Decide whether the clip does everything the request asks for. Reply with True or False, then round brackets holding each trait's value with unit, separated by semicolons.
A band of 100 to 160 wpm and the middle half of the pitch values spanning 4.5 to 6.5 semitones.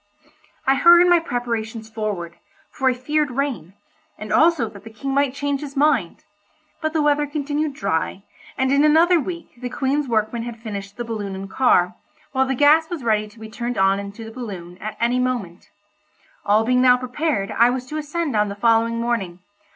False (190 wpm; 5.0 semitones)